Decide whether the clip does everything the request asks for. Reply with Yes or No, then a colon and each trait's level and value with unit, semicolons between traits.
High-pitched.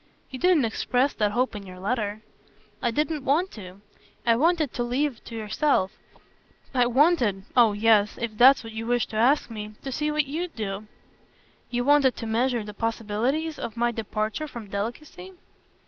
Yes: high, 240 Hz